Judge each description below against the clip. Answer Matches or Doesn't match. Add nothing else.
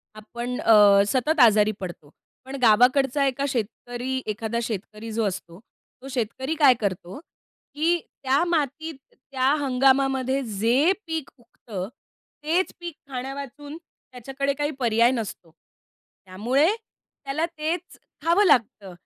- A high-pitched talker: Matches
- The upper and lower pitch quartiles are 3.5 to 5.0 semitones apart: Matches